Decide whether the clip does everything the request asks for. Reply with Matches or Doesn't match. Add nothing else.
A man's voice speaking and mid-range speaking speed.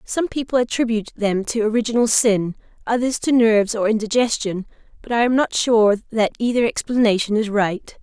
Doesn't match